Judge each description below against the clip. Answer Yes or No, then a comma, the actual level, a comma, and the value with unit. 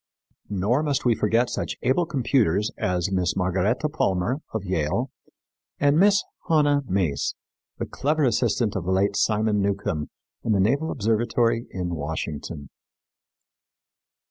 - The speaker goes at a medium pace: No, slow, 130 wpm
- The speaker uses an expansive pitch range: Yes, wide, 6.0 semitones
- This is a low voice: Yes, low, 105 Hz